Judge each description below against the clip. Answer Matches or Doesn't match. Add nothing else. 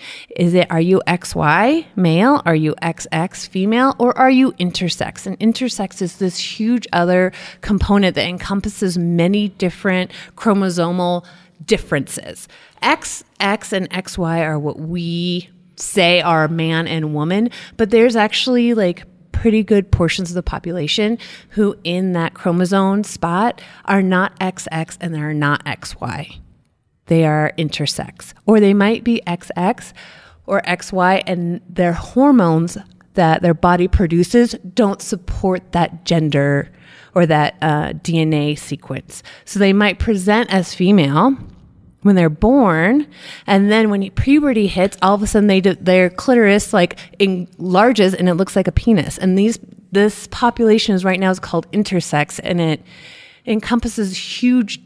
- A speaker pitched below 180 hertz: Doesn't match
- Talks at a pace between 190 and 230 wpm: Doesn't match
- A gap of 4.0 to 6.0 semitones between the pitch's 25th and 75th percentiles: Doesn't match